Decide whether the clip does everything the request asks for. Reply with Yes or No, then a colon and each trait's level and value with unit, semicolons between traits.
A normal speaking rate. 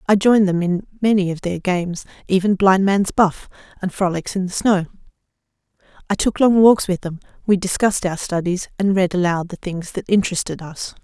Yes: average, 190 wpm